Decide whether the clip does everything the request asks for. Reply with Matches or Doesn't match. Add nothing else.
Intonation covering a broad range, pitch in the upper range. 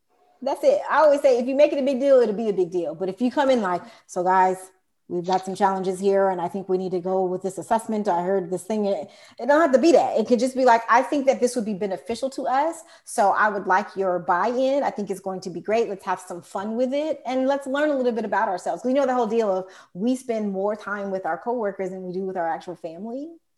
Matches